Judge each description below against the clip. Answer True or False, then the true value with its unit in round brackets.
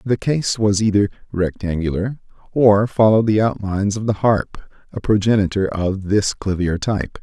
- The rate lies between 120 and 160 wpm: True (150 wpm)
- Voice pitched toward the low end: True (105 Hz)